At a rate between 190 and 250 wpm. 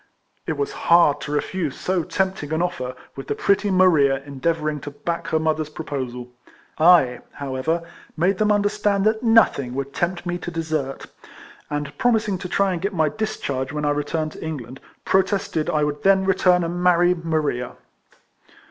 No: average, 165 wpm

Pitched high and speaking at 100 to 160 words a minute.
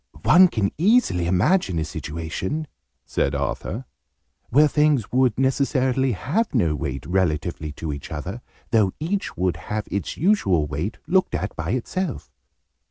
No: low, 105 Hz; average, 140 wpm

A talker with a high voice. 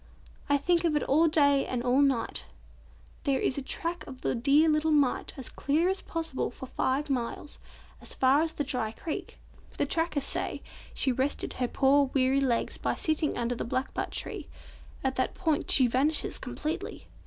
Yes: very high, 280 Hz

